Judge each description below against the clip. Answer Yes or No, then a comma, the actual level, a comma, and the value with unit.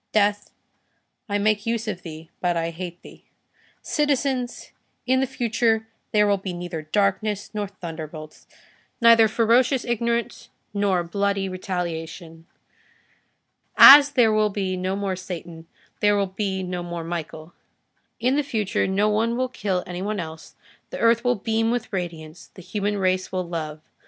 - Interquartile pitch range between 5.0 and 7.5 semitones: No, average, 4.3 semitones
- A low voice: No, high, 200 Hz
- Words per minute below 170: Yes, average, 150 wpm